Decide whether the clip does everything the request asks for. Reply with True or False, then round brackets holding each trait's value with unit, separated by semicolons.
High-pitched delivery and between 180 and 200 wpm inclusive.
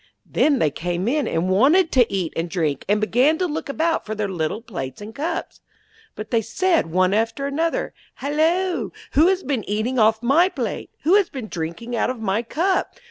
True (235 Hz; 195 wpm)